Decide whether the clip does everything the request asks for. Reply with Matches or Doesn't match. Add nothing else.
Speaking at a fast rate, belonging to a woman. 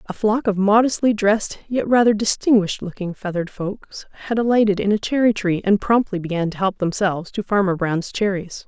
Doesn't match